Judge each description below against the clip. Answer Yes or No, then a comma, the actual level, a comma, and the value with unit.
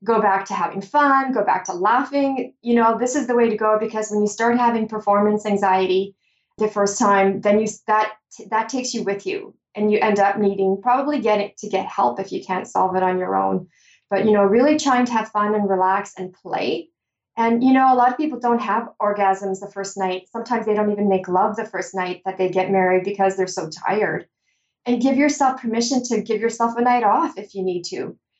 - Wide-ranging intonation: No, average, 3.6 semitones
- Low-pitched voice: No, high, 210 Hz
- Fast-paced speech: Yes, fast, 230 wpm